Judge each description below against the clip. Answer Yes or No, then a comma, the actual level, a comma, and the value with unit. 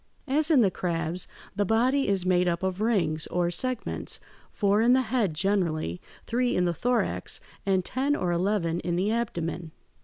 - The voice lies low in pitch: No, high, 190 Hz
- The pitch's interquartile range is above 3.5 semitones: Yes, wide, 5.4 semitones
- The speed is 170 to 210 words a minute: Yes, average, 175 wpm